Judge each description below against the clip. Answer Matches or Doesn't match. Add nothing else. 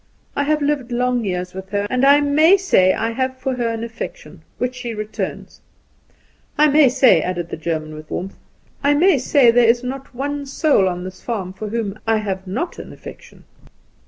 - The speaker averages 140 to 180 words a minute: Doesn't match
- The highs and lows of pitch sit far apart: Matches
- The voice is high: Matches